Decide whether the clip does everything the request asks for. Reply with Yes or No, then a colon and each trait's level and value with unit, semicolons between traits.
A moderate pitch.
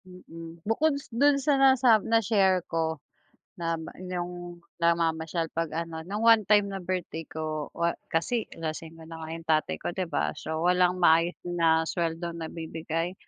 Yes: medium, 170 Hz